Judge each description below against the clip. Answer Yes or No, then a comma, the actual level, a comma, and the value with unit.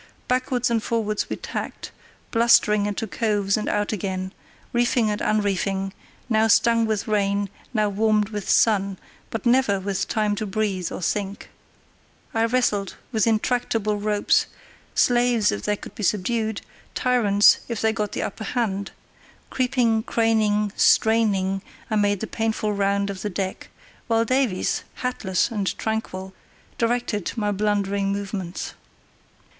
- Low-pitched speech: No, high, 210 Hz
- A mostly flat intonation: Yes, narrow, 2.2 semitones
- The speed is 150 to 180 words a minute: No, average, 140 wpm